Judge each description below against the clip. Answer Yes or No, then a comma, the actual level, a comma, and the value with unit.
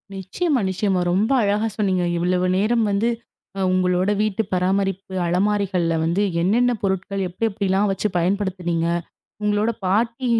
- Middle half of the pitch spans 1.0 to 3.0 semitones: Yes, narrow, 2.4 semitones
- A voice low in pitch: No, high, 195 Hz